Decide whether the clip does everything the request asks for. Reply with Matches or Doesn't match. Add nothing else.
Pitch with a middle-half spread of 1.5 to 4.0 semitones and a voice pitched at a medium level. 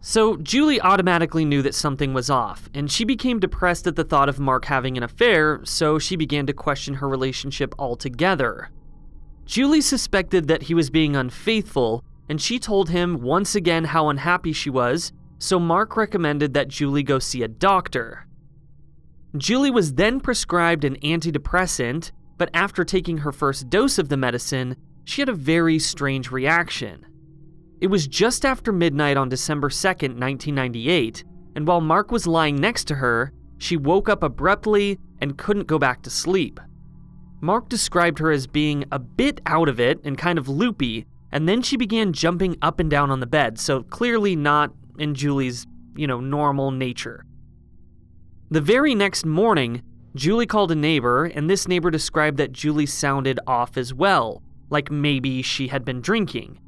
Doesn't match